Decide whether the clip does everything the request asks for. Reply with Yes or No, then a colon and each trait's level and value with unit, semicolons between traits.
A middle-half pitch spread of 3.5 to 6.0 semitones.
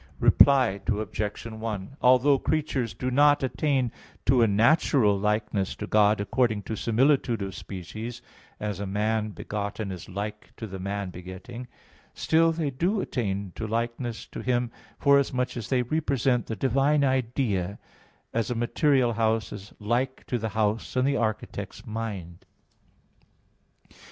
Yes: average, 3.9 semitones